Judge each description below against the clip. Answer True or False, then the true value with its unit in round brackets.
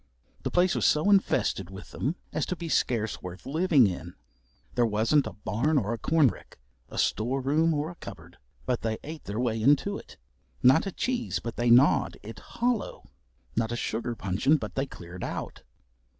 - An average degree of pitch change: False (6.3 semitones)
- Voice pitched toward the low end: True (125 Hz)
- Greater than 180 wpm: True (190 wpm)